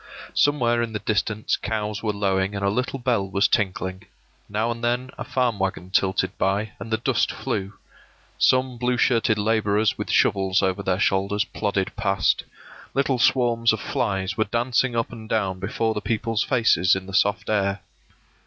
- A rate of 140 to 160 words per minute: No, average, 170 wpm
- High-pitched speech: No, low, 105 Hz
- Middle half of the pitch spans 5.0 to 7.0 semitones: No, average, 3.2 semitones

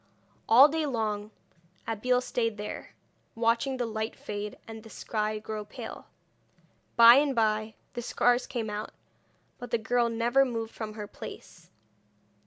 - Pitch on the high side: Yes, high, 225 Hz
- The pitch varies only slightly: Yes, narrow, 2.2 semitones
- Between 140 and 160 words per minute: Yes, average, 145 wpm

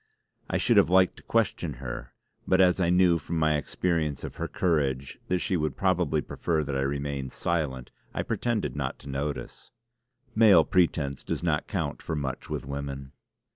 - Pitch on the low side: Yes, very low, 75 Hz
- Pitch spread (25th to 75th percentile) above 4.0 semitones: Yes, average, 4.4 semitones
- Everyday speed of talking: Yes, average, 175 wpm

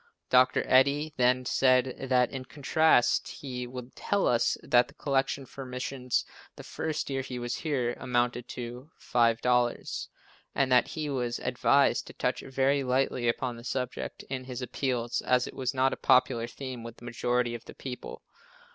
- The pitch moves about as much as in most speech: No, narrow, 1.6 semitones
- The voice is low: Yes, low, 125 Hz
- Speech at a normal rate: Yes, average, 170 wpm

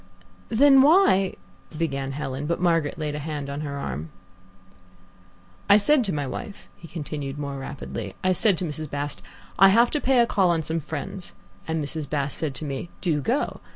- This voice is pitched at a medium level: Yes, medium, 155 Hz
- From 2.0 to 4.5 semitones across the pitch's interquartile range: No, average, 5.1 semitones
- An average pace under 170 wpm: No, average, 190 wpm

